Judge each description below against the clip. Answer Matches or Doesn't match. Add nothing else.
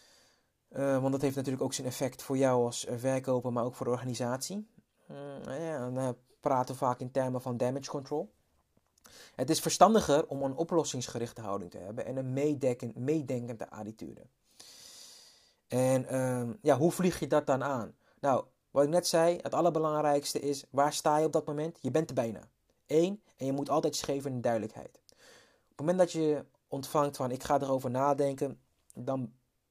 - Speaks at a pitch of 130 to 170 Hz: Matches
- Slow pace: Doesn't match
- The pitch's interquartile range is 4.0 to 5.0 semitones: Doesn't match